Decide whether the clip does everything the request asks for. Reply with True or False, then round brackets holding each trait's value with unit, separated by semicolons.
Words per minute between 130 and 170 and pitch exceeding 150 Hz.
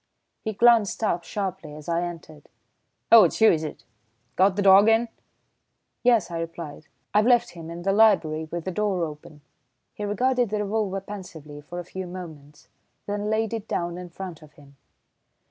False (180 wpm; 185 Hz)